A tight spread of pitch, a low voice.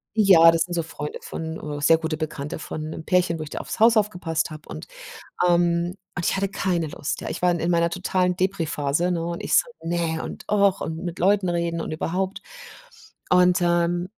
No: narrow, 2.0 semitones; medium, 170 Hz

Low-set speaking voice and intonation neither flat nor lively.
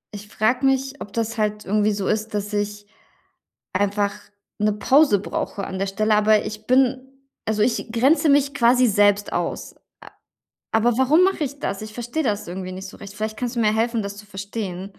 No: high, 215 Hz; average, 3.1 semitones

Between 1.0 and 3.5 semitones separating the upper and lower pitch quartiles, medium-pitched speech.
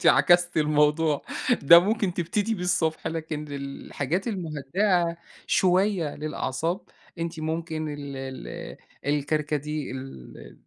Yes: average, 3.2 semitones; medium, 160 Hz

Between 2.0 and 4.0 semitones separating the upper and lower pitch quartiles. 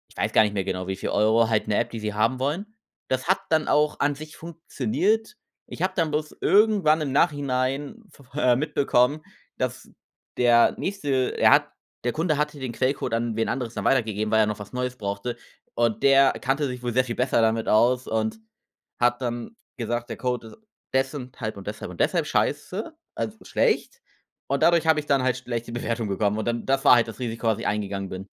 No: average, 4.7 semitones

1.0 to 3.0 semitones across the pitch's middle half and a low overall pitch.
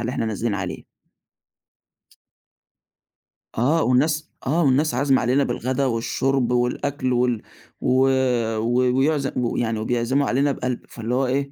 Yes: narrow, 2.5 semitones; low, 125 Hz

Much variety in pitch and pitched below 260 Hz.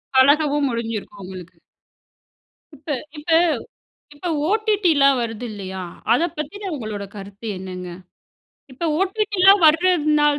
No: wide, 8.8 semitones; very high, 285 Hz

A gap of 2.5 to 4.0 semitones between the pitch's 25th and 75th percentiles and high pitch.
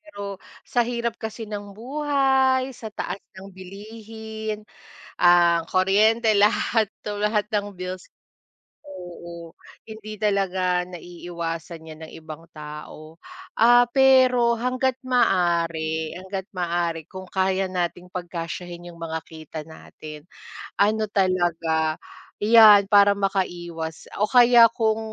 No: average, 4.4 semitones; high, 195 Hz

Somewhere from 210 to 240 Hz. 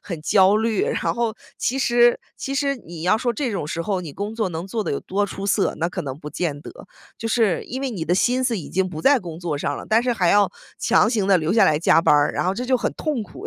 No: high, 200 Hz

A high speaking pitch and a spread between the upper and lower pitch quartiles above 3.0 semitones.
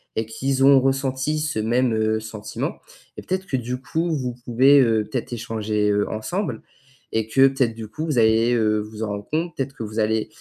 No: low, 120 Hz; average, 3.6 semitones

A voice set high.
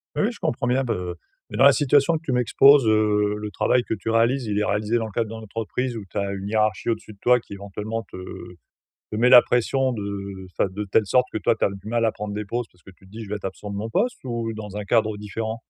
No: low, 110 Hz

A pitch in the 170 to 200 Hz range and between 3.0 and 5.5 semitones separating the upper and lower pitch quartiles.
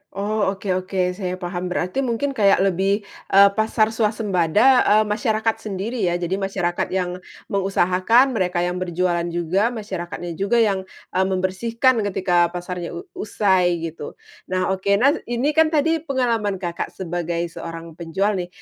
Yes: high, 190 Hz; average, 3.4 semitones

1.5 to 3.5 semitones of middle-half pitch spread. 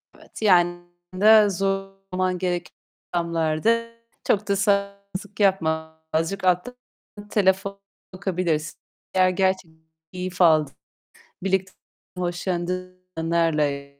Yes: narrow, 2.6 semitones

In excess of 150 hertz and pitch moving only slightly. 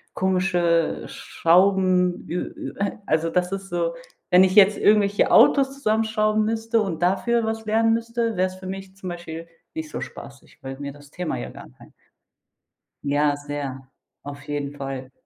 No: medium, 185 Hz; wide, 5.7 semitones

